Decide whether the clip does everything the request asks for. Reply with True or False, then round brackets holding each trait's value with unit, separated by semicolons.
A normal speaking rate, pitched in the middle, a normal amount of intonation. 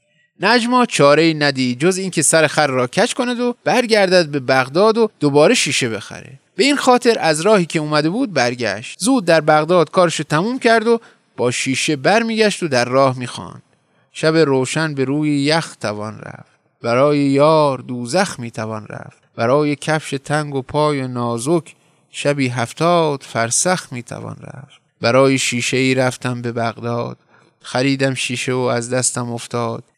False (160 wpm; 145 Hz; 5.0 semitones)